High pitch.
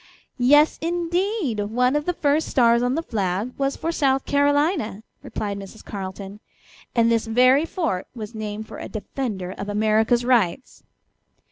Yes: high, 240 Hz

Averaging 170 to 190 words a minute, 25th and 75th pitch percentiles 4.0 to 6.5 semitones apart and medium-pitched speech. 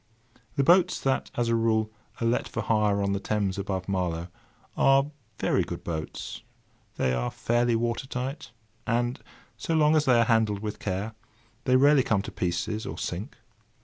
No: average, 175 wpm; average, 4.5 semitones; low, 115 Hz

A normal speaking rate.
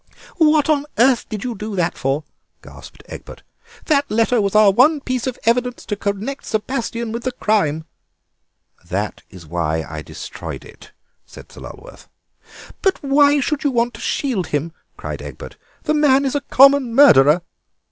Yes: average, 165 wpm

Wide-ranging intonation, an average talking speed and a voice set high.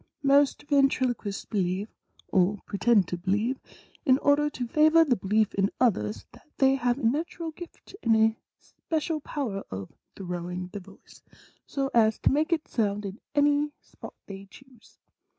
Yes: wide, 6.5 semitones; average, 155 wpm; high, 235 Hz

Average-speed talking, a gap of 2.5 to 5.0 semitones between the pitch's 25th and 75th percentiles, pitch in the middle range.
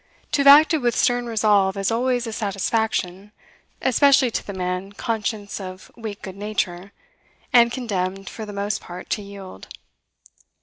No: average, 150 wpm; average, 3.4 semitones; high, 210 Hz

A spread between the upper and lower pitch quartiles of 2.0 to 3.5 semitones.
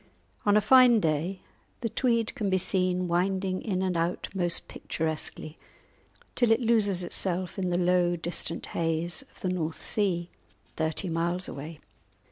Yes: average, 2.7 semitones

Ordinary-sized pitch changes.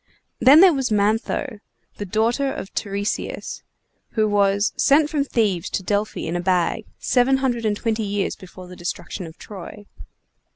Yes: average, 4.1 semitones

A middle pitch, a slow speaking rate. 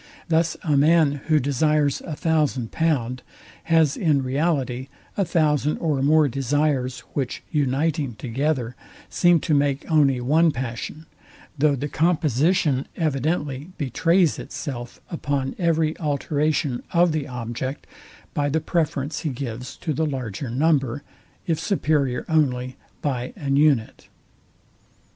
Yes: medium, 145 Hz; slow, 125 wpm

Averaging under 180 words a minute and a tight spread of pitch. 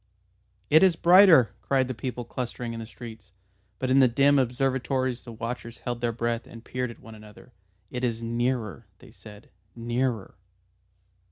Yes: average, 165 wpm; narrow, 2.1 semitones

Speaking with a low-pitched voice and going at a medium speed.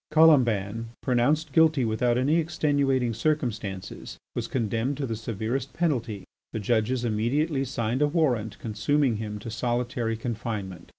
No: low, 120 Hz; slow, 130 wpm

